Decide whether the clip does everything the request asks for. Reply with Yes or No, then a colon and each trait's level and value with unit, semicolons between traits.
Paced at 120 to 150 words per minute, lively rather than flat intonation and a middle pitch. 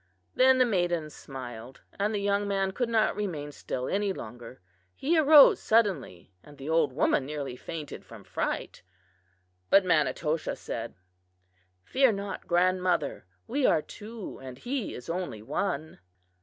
Yes: average, 140 wpm; wide, 6.4 semitones; medium, 180 Hz